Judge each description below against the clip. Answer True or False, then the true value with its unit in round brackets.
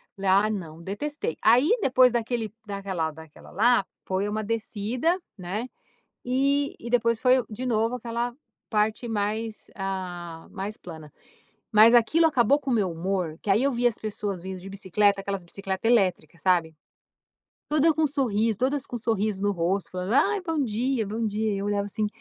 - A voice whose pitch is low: False (215 Hz)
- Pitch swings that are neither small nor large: True (4.0 semitones)